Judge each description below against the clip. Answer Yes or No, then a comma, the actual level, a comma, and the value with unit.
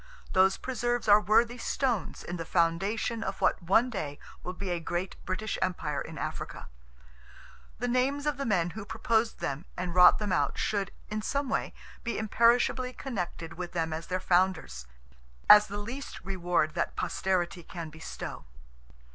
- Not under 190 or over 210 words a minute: No, average, 165 wpm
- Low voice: No, high, 190 Hz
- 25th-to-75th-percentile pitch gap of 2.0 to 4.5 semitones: No, average, 5.0 semitones